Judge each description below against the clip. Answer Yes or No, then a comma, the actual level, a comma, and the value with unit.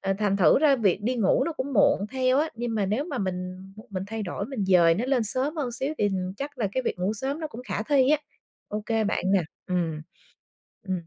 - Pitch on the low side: No, high, 220 Hz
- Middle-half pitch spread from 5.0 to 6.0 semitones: Yes, wide, 5.6 semitones